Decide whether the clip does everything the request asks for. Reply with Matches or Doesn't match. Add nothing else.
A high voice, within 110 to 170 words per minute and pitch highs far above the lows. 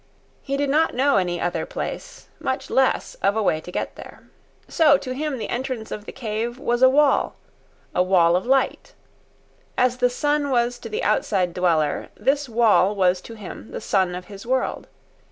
Doesn't match